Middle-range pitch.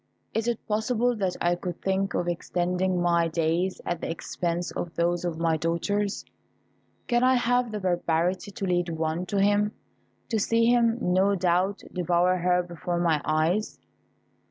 Yes: medium, 180 Hz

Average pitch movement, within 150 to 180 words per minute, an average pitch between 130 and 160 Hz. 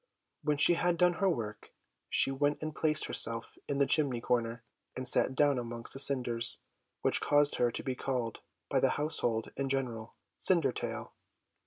Yes: average, 3.8 semitones; average, 170 wpm; low, 135 Hz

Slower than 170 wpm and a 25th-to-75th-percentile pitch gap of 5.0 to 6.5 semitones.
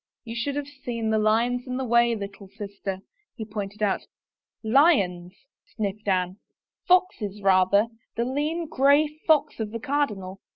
No: average, 175 wpm; average, 5.3 semitones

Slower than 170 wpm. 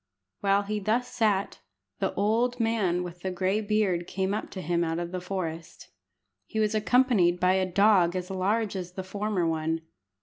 No: average, 180 wpm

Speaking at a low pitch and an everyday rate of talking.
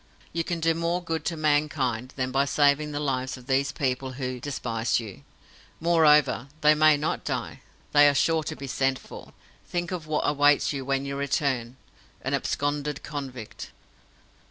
No: medium, 145 Hz; average, 170 wpm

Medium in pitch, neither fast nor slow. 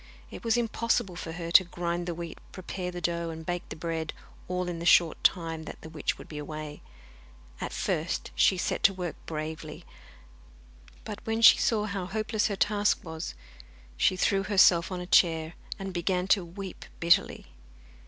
Yes: medium, 175 Hz; average, 180 wpm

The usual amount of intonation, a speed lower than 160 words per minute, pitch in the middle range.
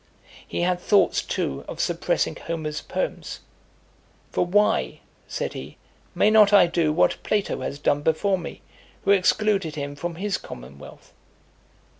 Yes: average, 4.7 semitones; average, 140 wpm; medium, 175 Hz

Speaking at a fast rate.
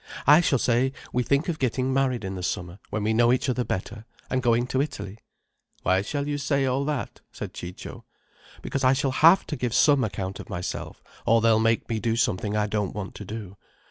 Yes: fast, 215 wpm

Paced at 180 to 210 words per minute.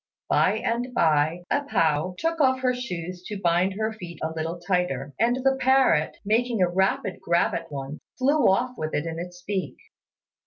Yes: average, 185 wpm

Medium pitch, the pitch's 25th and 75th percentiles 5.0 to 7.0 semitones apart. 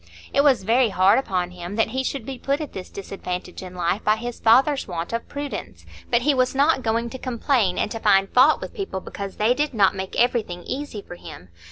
No: high, 225 Hz; wide, 5.6 semitones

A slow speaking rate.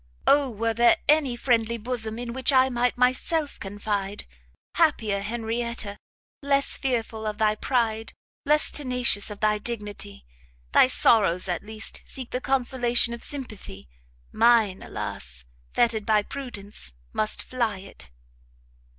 Yes: slow, 130 wpm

